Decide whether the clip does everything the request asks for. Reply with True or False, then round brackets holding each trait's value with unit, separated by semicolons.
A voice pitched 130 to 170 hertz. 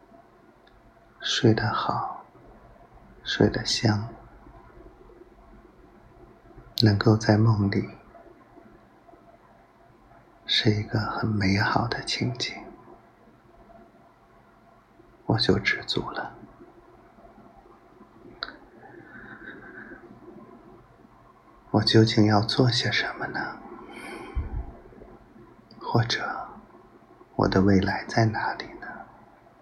False (110 Hz)